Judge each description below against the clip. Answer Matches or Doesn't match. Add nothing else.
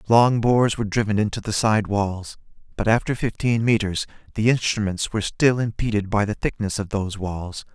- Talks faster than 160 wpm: Matches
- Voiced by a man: Matches